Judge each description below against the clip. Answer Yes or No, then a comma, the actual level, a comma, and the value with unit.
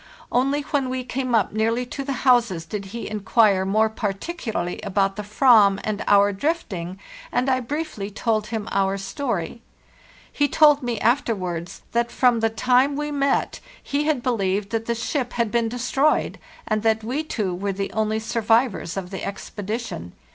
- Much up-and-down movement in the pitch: No, average, 4.1 semitones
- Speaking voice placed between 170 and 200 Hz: No, high, 225 Hz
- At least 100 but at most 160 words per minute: No, average, 170 wpm